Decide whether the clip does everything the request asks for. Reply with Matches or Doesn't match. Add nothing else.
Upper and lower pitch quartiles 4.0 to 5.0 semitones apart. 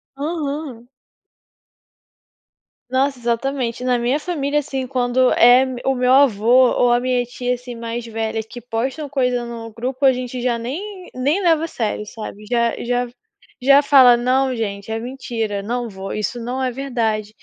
Doesn't match